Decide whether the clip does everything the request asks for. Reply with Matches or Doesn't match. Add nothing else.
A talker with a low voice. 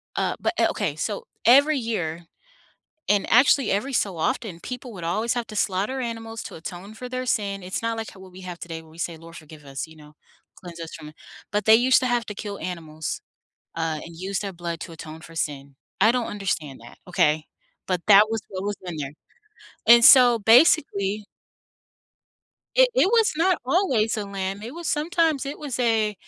Doesn't match